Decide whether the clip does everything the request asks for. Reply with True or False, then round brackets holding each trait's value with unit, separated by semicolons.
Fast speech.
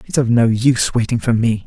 True (250 wpm)